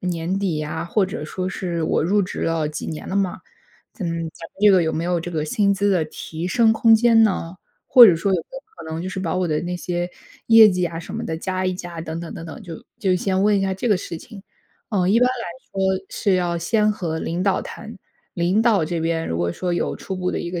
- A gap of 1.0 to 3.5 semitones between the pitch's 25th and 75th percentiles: Yes, average, 3.0 semitones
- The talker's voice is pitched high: No, medium, 180 Hz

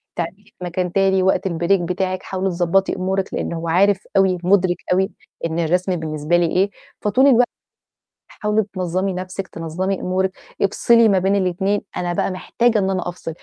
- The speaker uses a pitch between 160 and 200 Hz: Yes, medium, 185 Hz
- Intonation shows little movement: Yes, narrow, 1.8 semitones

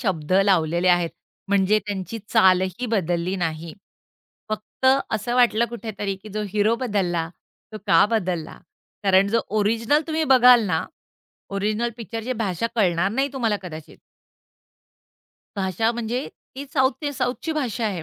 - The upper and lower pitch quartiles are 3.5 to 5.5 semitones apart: Yes, average, 4.2 semitones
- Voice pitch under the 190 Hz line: No, high, 210 Hz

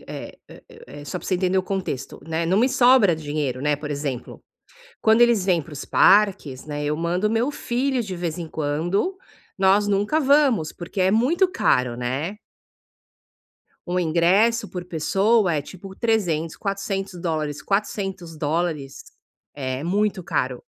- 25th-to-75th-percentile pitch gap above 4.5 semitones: Yes, average, 5.2 semitones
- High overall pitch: No, medium, 180 Hz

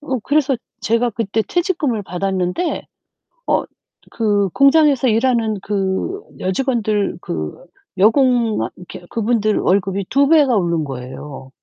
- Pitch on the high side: Yes, high, 220 Hz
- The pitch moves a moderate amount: No, wide, 5.8 semitones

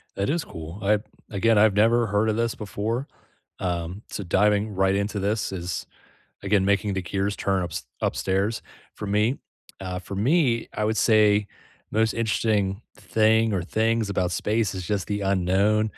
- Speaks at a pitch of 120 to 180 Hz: No, low, 105 Hz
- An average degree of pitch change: No, narrow, 2.3 semitones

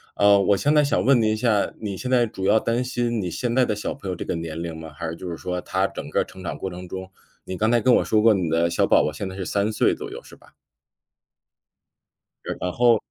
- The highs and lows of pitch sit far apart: No, average, 4.3 semitones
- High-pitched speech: No, low, 100 Hz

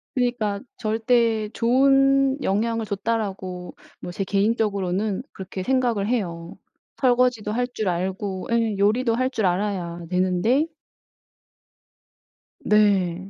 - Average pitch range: Yes, average, 4.1 semitones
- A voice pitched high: Yes, high, 210 Hz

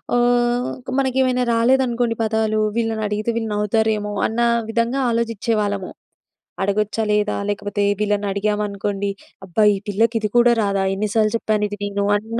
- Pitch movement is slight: Yes, narrow, 2.1 semitones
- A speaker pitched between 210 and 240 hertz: Yes, high, 215 Hz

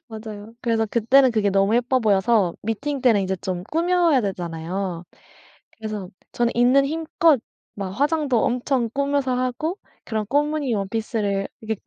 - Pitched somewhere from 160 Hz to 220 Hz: No, high, 230 Hz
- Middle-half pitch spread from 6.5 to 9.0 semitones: No, average, 5.3 semitones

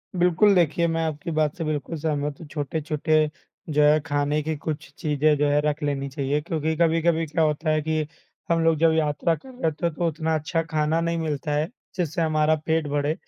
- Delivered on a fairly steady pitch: Yes, narrow, 1.7 semitones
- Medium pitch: Yes, medium, 155 Hz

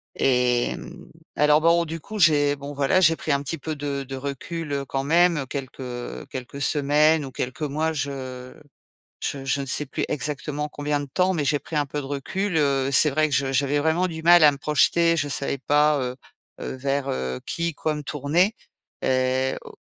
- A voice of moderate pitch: Yes, medium, 145 Hz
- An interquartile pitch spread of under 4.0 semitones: Yes, narrow, 2.5 semitones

